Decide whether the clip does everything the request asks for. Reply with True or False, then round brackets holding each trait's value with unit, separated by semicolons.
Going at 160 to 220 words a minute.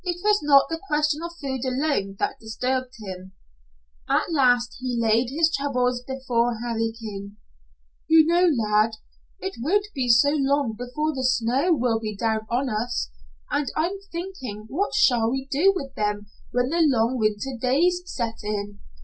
True (165 wpm)